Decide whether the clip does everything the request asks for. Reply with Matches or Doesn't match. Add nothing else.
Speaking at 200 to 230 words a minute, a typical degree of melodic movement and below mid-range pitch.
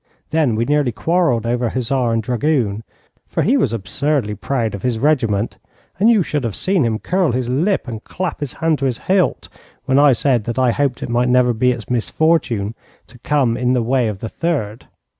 Matches